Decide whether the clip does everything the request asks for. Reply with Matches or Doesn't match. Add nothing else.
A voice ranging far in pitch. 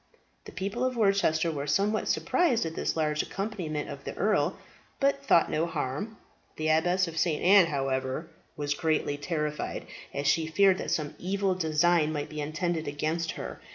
Doesn't match